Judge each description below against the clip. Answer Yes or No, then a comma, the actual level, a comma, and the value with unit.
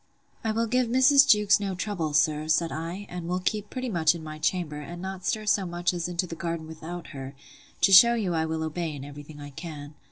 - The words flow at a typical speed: No, fast, 235 wpm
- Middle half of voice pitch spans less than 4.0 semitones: No, average, 4.3 semitones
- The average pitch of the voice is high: No, medium, 175 Hz